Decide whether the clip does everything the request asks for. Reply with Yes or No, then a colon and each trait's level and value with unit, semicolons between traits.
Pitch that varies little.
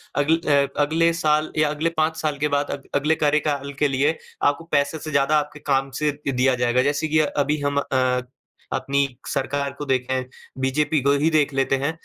Yes: narrow, 1.9 semitones